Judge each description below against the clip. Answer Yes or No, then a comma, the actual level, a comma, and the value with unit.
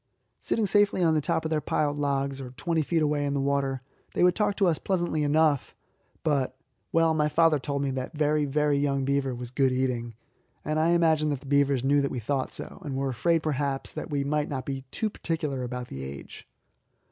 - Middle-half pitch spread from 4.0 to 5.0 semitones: No, average, 2.7 semitones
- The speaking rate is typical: No, fast, 215 wpm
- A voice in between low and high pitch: Yes, medium, 145 Hz